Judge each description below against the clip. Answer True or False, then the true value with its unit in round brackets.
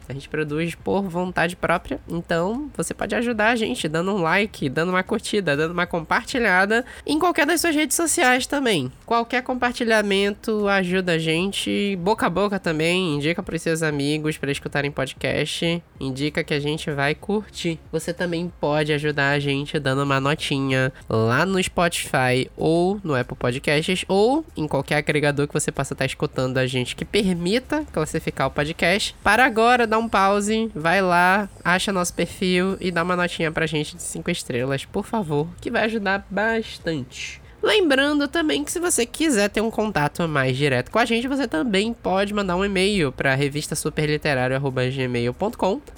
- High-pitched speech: False (170 Hz)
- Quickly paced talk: False (170 wpm)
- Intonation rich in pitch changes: True (6.1 semitones)